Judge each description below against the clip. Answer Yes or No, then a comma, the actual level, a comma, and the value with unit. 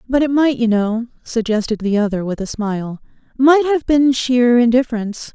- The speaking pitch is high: Yes, high, 240 Hz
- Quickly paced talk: No, average, 170 wpm